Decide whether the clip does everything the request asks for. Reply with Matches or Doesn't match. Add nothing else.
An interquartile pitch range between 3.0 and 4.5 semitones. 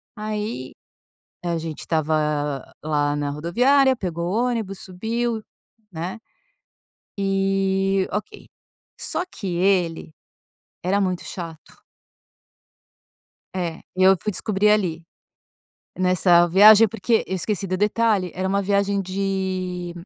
Matches